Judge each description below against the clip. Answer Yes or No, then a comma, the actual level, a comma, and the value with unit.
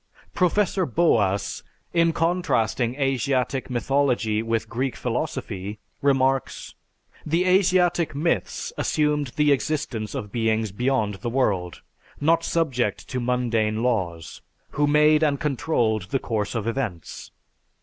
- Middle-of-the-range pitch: No, low, 130 Hz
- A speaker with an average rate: No, slow, 115 wpm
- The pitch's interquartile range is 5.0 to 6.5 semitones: Yes, average, 5.3 semitones